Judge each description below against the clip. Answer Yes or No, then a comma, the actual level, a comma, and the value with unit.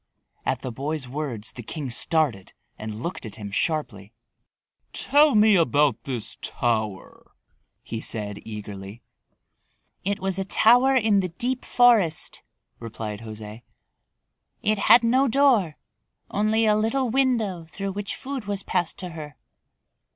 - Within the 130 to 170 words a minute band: Yes, slow, 135 wpm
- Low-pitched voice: No, medium, 165 Hz